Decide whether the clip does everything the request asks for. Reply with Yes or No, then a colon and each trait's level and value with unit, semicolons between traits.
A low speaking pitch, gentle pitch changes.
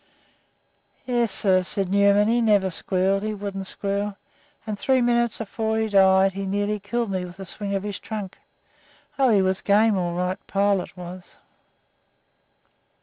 No: high, 200 Hz; narrow, 2.1 semitones